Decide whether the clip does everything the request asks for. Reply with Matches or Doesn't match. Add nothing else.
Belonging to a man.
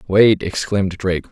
Matches